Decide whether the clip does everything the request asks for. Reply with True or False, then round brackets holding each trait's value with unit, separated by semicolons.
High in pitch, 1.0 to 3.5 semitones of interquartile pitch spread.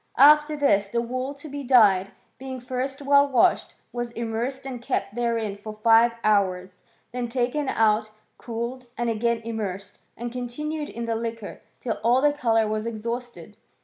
True (235 Hz; 2.8 semitones)